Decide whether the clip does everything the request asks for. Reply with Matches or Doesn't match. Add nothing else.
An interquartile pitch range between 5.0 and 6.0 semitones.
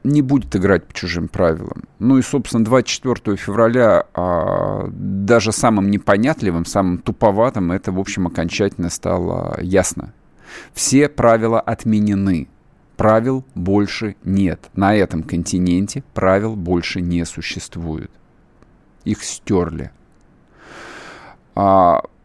Doesn't match